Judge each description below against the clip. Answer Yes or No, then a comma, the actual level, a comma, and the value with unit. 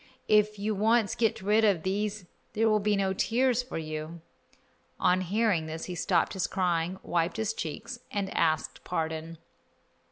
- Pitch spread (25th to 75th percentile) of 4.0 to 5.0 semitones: Yes, average, 4.3 semitones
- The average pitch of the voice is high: Yes, high, 195 Hz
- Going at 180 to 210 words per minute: No, average, 160 wpm